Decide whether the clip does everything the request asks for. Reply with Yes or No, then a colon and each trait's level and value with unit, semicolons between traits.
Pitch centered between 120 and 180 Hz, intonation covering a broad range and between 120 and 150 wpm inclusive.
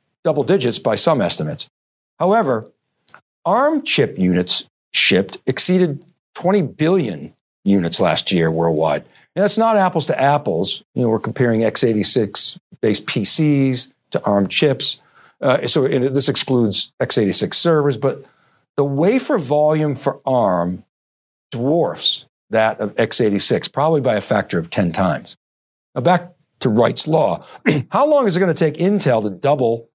Yes: medium, 140 Hz; wide, 8.3 semitones; average, 140 wpm